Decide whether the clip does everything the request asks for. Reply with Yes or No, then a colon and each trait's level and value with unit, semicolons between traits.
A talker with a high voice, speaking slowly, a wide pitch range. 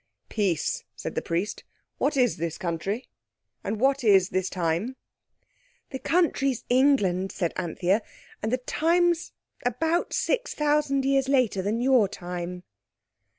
Yes: high, 230 Hz; slow, 130 wpm; wide, 6.8 semitones